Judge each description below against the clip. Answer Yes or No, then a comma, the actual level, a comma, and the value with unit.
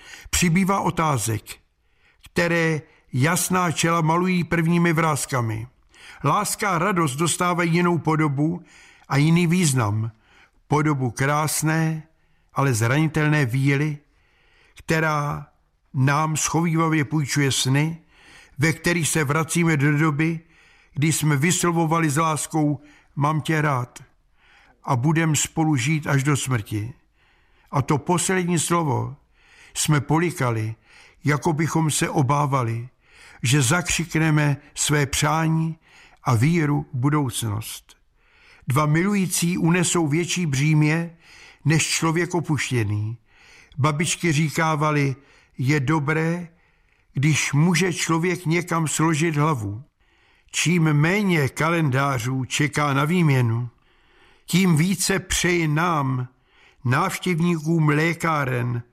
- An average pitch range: Yes, average, 3.1 semitones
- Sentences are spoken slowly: Yes, slow, 100 wpm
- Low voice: No, medium, 155 Hz